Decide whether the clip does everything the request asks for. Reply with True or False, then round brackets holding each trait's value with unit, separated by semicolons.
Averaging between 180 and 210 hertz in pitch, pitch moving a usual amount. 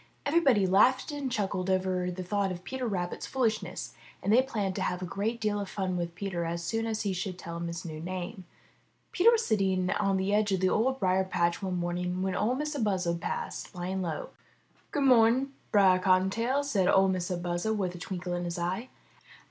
True (190 Hz; 3.6 semitones)